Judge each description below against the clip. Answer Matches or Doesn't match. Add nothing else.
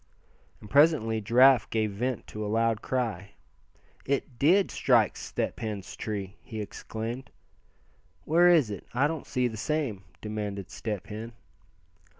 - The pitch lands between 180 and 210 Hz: Doesn't match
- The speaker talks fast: Doesn't match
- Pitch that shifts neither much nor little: Matches